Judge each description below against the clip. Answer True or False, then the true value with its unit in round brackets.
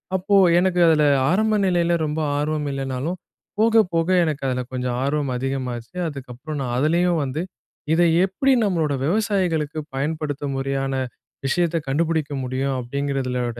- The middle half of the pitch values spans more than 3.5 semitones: True (4.2 semitones)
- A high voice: False (150 Hz)